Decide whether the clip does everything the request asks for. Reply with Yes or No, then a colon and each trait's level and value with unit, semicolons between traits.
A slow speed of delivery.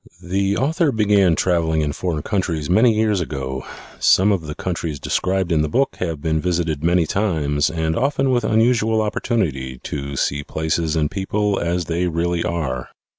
No: average, 170 wpm